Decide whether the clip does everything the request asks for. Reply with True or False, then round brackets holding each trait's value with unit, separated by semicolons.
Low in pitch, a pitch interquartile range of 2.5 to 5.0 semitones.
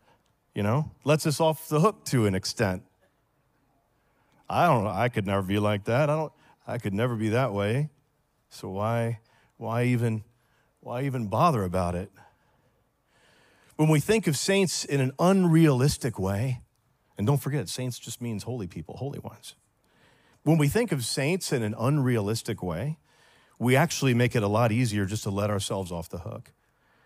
False (125 Hz; 5.4 semitones)